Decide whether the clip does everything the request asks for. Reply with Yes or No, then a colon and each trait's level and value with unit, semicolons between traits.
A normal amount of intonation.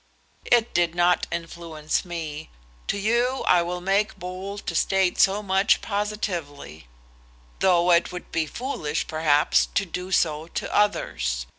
Yes: average, 3.8 semitones